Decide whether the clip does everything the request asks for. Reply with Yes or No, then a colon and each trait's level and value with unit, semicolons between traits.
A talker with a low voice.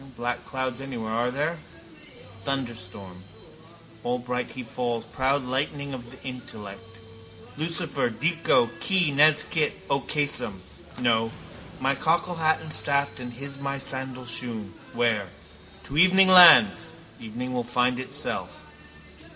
Yes: low, 130 Hz